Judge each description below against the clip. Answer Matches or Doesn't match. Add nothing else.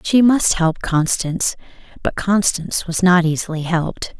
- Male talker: Doesn't match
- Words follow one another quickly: Doesn't match